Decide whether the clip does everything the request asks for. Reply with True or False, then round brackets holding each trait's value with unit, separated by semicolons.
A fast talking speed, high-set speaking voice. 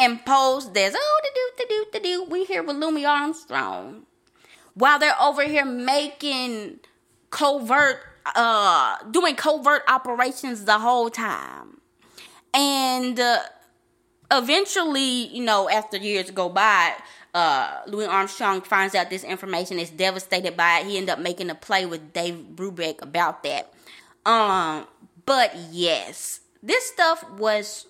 False (135 wpm; 250 Hz)